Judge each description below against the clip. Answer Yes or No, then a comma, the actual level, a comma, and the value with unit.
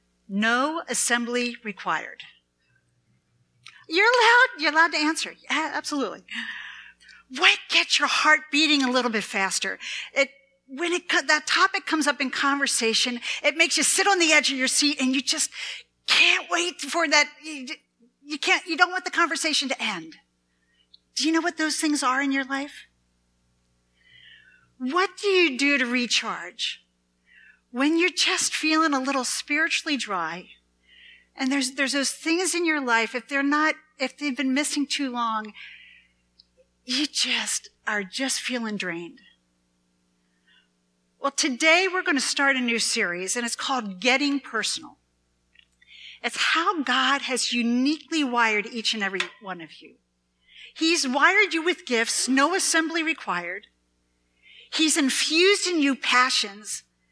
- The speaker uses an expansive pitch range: Yes, wide, 6.8 semitones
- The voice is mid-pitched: No, very high, 270 Hz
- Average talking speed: Yes, average, 150 wpm